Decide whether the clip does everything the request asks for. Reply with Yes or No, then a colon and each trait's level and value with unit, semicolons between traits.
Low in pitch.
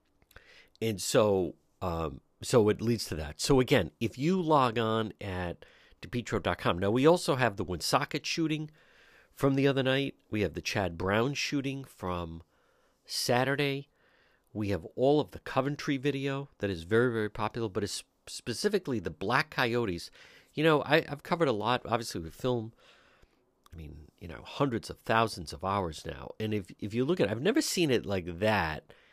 Yes: low, 115 Hz